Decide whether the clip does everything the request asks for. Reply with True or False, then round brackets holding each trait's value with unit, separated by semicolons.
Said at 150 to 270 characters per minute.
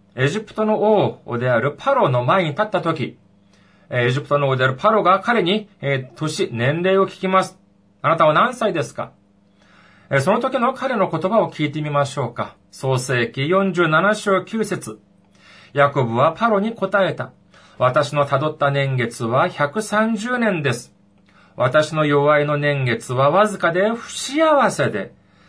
True (255 characters per minute)